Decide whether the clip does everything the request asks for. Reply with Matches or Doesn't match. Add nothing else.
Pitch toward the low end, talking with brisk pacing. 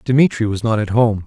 Matches